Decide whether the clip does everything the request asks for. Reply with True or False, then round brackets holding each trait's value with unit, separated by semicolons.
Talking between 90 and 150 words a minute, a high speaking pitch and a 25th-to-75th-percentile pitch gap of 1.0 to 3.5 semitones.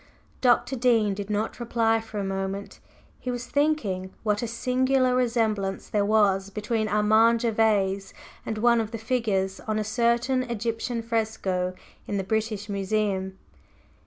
True (145 wpm; 220 Hz; 2.8 semitones)